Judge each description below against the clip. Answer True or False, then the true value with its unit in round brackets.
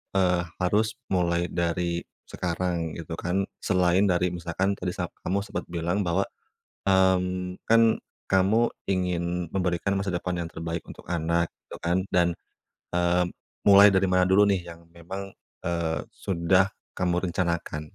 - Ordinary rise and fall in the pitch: False (1.7 semitones)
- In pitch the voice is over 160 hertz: False (90 Hz)